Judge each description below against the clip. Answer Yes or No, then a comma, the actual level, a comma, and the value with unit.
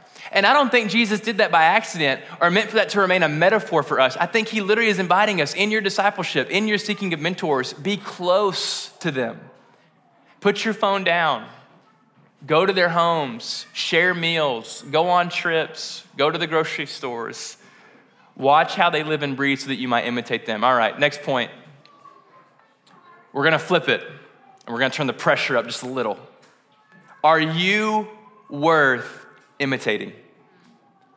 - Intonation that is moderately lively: Yes, average, 4.9 semitones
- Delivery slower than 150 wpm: No, average, 175 wpm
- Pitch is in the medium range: Yes, medium, 180 Hz